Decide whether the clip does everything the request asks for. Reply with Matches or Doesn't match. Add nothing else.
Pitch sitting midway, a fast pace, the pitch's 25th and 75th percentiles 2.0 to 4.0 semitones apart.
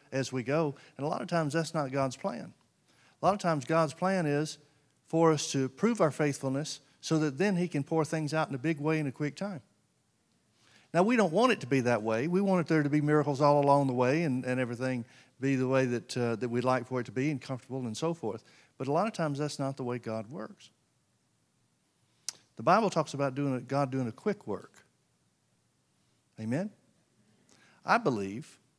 Matches